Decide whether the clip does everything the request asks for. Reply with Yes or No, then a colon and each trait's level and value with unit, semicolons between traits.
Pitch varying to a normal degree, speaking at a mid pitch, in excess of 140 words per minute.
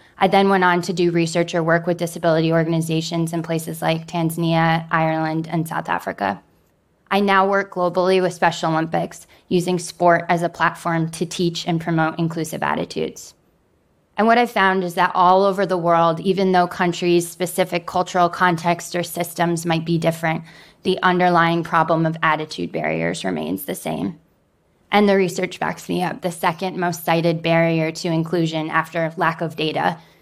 No: narrow, 1.8 semitones; medium, 170 Hz; average, 170 wpm